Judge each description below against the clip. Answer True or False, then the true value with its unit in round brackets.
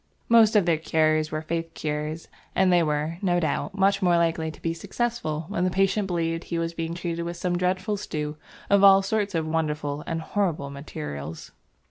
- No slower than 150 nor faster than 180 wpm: False (190 wpm)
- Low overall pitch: False (165 Hz)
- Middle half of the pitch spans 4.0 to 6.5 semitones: False (3.4 semitones)